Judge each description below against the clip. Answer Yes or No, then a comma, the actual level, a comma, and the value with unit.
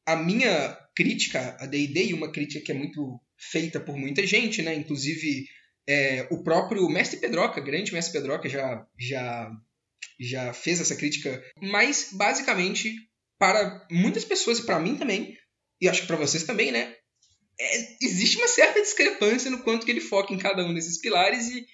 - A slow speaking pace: No, average, 175 wpm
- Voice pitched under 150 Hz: No, medium, 165 Hz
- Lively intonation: Yes, wide, 6.4 semitones